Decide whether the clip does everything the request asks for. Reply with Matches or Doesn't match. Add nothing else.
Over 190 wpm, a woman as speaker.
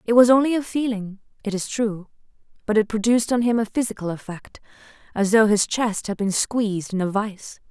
Matches